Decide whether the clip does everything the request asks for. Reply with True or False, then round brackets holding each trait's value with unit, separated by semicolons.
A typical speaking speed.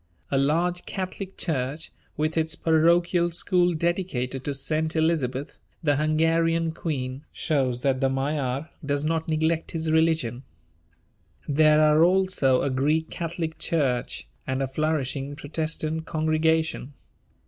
False (125 wpm)